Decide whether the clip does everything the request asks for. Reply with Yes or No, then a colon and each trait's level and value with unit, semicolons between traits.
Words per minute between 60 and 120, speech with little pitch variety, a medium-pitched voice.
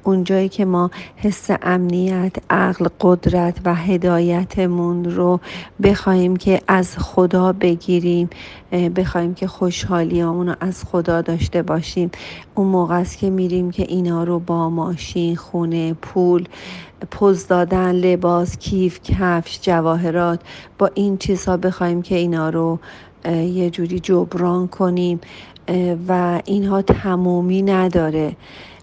Yes: average, 115 wpm; narrow, 1.2 semitones; medium, 180 Hz